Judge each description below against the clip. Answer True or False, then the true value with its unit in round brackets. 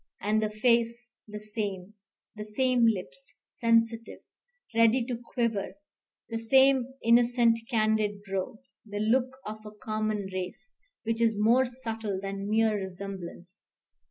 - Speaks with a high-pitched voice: True (220 Hz)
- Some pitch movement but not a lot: False (2.2 semitones)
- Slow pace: True (130 wpm)